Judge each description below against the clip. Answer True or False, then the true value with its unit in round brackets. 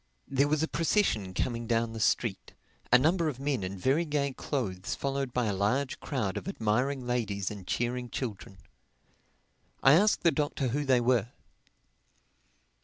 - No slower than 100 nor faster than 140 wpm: False (160 wpm)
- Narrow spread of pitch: False (4.2 semitones)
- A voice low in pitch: True (125 Hz)